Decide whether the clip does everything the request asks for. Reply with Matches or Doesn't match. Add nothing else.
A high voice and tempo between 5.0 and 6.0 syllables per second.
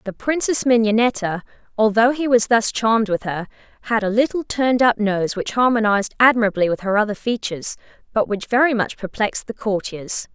Matches